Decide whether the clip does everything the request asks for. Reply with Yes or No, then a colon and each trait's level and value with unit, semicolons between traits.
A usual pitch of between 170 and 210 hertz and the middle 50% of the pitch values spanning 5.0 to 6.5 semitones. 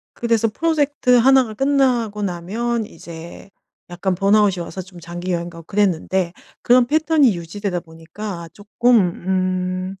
Yes: high, 200 Hz; average, 5.3 semitones